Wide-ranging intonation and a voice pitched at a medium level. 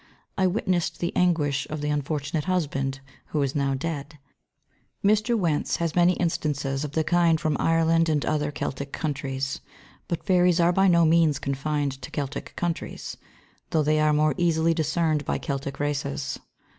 No: average, 3.0 semitones; medium, 155 Hz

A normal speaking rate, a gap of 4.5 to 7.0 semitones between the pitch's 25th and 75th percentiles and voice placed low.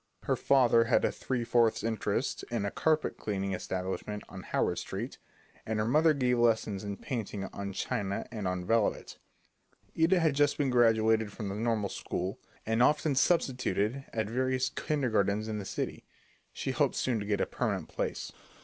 No: average, 170 wpm; average, 4.1 semitones; low, 115 Hz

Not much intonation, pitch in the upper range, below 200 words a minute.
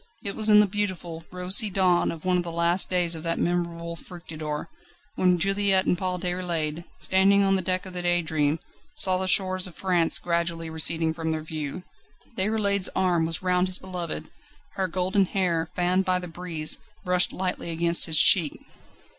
No: narrow, 2.0 semitones; medium, 180 Hz; average, 180 wpm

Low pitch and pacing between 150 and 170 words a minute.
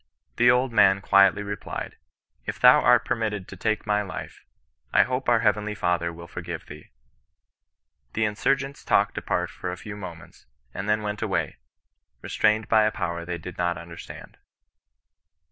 Yes: low, 105 Hz; average, 160 wpm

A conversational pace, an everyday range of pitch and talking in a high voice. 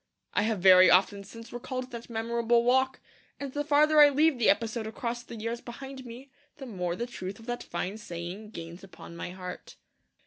Yes: average, 195 wpm; average, 4.7 semitones; high, 230 Hz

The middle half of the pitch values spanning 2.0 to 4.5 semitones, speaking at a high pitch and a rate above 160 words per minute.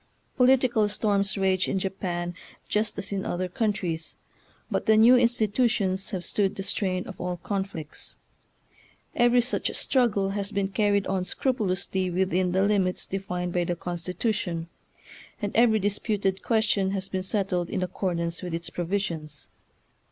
No: narrow, 2.6 semitones; high, 195 Hz; average, 145 wpm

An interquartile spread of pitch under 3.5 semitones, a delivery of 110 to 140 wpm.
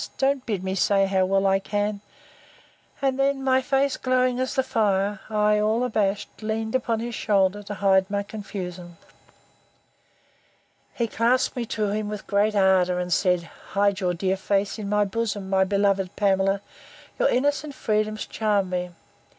No: average, 2.8 semitones; average, 160 wpm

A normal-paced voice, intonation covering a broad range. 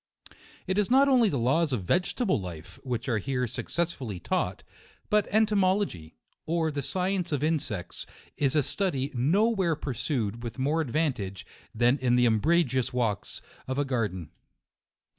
Yes: average, 155 wpm; wide, 6.7 semitones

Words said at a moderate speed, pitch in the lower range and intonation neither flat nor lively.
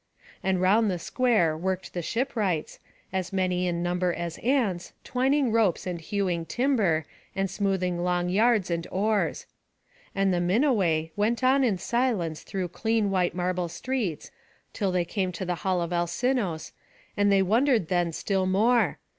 No: average, 155 wpm; high, 190 Hz; average, 4.0 semitones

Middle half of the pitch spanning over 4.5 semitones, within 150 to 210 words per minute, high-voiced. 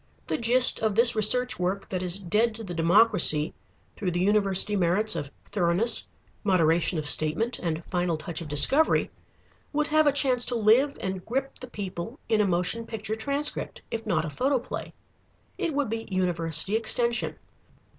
Yes: average, 5.0 semitones; average, 165 wpm; high, 210 Hz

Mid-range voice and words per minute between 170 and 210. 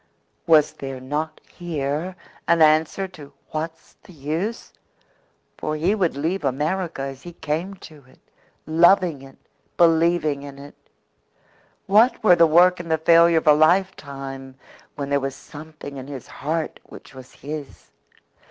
No: medium, 155 Hz; average, 145 wpm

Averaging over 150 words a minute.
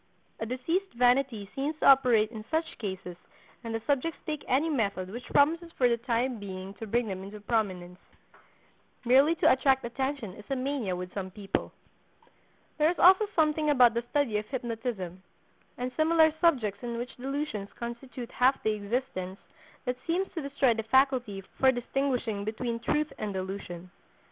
Yes: average, 165 wpm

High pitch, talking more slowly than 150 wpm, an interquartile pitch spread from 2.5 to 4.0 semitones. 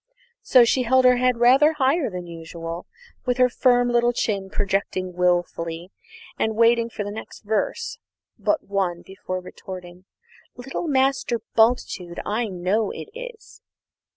No: high, 220 Hz; average, 140 wpm; wide, 5.4 semitones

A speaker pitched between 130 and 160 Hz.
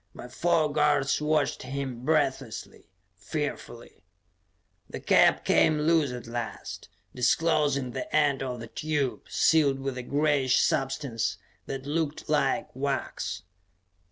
Yes: medium, 140 Hz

